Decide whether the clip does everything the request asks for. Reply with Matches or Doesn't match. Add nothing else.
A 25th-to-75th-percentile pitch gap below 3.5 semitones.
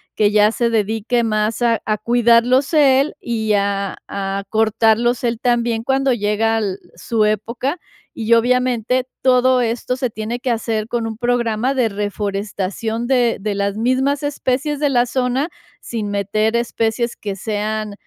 Matches